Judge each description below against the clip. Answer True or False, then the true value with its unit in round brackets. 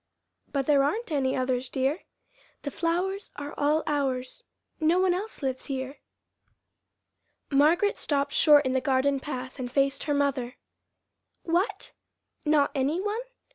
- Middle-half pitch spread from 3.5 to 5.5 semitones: True (3.9 semitones)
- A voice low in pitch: False (285 Hz)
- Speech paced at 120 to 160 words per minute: True (135 wpm)